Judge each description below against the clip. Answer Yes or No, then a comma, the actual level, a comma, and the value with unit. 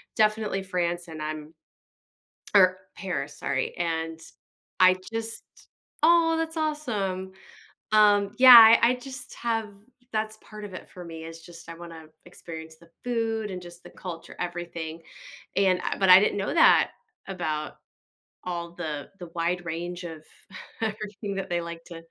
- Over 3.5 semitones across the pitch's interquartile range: Yes, average, 4.2 semitones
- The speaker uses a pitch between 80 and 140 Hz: No, medium, 180 Hz